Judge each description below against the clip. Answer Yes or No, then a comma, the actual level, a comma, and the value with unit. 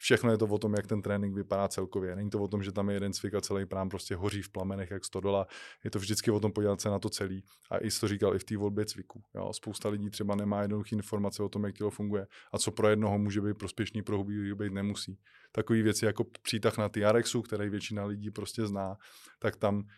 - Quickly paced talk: Yes, fast, 250 wpm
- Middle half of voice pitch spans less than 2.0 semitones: Yes, narrow, 1.1 semitones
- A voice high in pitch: No, low, 105 Hz